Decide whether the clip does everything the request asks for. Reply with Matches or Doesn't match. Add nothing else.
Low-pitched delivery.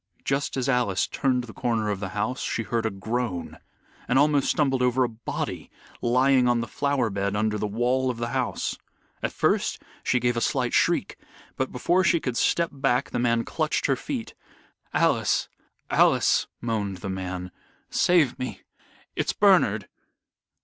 Matches